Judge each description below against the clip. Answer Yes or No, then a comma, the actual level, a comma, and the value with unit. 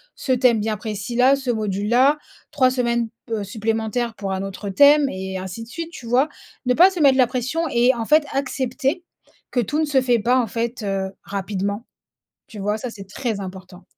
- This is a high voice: Yes, high, 235 Hz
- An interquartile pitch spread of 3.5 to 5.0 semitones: Yes, average, 4.4 semitones